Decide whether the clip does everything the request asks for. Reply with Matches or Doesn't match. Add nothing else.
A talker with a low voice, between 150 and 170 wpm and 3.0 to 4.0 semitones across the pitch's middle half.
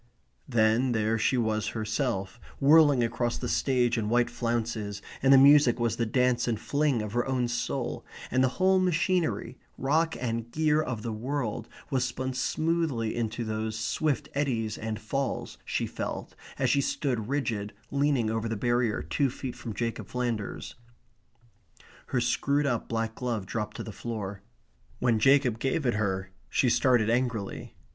Matches